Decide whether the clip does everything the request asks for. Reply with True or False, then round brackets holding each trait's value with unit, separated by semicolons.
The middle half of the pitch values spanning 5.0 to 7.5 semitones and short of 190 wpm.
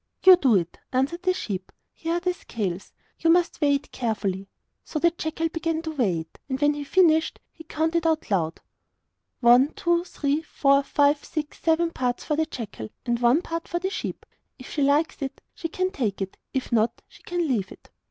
False (5.5 semitones; 205 wpm)